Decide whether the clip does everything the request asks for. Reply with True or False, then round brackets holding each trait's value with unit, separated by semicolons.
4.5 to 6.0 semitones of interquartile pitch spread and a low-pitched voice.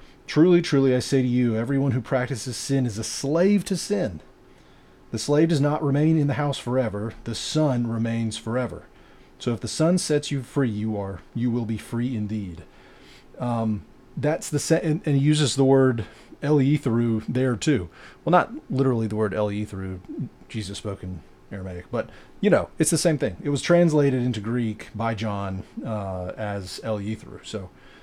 True (4.9 semitones; 120 Hz)